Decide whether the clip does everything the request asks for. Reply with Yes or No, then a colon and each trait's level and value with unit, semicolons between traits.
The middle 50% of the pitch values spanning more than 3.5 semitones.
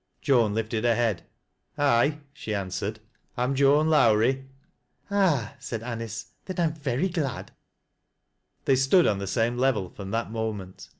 Yes: average, 4.4 semitones